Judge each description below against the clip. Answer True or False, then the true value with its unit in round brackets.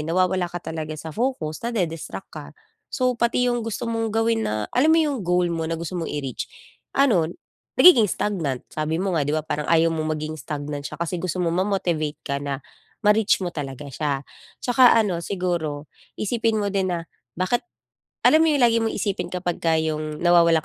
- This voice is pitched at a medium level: True (175 Hz)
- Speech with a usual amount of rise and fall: False (6.1 semitones)